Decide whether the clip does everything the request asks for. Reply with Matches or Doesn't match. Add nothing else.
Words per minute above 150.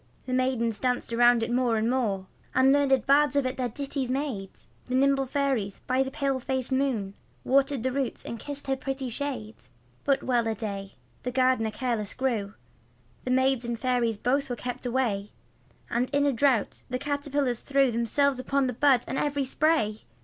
Matches